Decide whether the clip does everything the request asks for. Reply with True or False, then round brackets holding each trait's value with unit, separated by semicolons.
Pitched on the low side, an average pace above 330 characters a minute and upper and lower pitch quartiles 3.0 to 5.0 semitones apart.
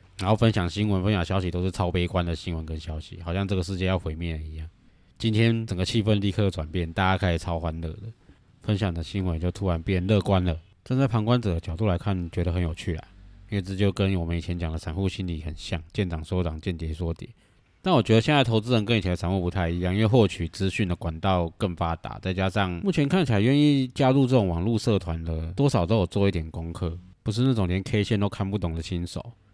True (95 Hz; 360 characters per minute; 3.8 semitones)